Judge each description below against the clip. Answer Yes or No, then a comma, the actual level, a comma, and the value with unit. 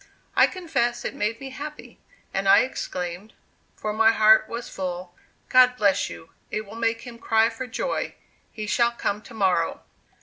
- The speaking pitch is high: Yes, high, 225 Hz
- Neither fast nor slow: Yes, average, 170 wpm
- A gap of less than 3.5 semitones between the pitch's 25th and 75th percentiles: Yes, average, 3.1 semitones